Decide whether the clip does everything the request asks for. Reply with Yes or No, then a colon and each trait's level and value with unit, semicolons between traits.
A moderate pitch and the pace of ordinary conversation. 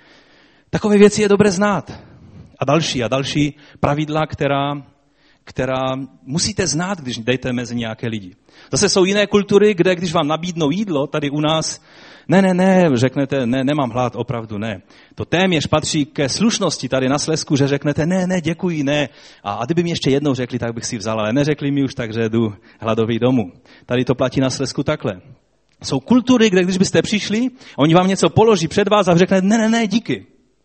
No: medium, 145 Hz; fast, 190 wpm